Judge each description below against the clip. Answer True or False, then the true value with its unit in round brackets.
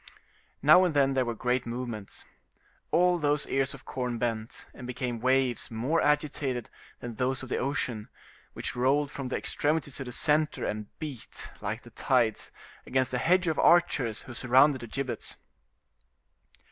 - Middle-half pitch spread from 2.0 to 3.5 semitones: True (3.2 semitones)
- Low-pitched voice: True (130 Hz)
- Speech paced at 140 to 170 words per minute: True (160 wpm)